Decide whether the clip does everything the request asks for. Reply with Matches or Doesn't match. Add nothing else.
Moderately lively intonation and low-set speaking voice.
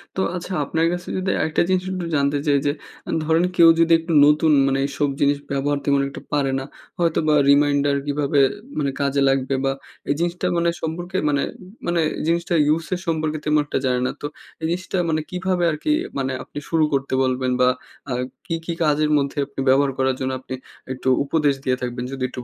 Doesn't match